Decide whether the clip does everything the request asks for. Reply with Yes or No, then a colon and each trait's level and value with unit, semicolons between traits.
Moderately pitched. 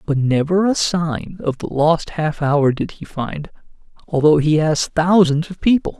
Yes: medium, 160 Hz